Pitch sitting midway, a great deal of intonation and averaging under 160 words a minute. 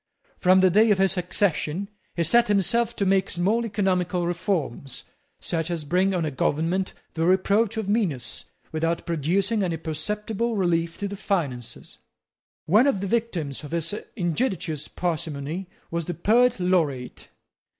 No: medium, 180 Hz; average, 3.6 semitones; average, 150 wpm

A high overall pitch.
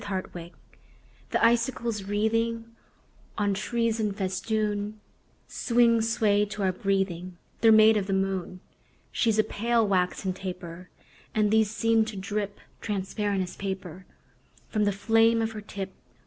Yes: high, 205 Hz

